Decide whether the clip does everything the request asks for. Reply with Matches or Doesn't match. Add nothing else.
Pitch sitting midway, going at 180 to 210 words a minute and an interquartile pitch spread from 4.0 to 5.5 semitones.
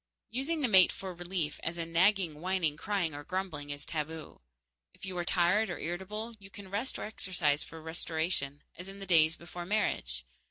Doesn't match